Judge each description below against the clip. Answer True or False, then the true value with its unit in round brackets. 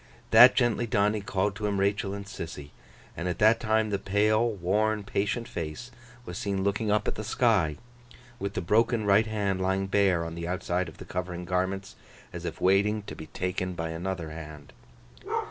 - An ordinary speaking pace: True (190 wpm)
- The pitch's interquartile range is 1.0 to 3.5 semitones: True (2.9 semitones)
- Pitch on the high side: False (100 Hz)